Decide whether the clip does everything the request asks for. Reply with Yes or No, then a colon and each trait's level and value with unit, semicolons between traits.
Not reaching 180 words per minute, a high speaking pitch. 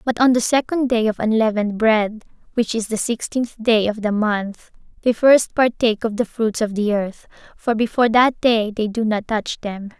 No: fast, 205 wpm; high, 225 Hz